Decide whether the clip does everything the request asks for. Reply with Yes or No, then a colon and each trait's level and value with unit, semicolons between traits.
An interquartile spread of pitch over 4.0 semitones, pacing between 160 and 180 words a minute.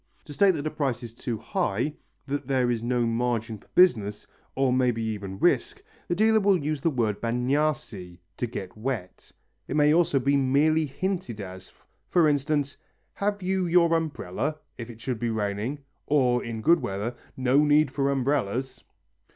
Yes: average, 5.0 semitones; average, 170 wpm